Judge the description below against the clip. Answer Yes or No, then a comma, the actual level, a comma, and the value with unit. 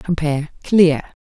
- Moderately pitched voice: Yes, medium, 160 Hz